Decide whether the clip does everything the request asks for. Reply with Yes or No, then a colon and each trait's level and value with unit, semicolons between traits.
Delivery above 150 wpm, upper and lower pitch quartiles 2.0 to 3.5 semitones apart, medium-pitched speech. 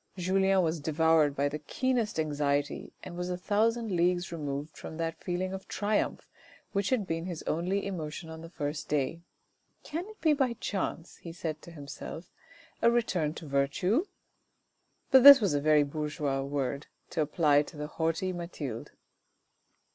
No: average, 160 wpm; average, 4.4 semitones; medium, 165 Hz